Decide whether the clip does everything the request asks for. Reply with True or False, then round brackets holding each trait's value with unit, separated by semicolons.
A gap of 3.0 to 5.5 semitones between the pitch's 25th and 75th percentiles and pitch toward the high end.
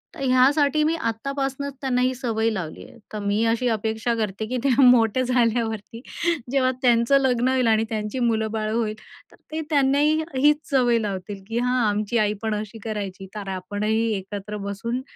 True (3.3 semitones; 230 Hz)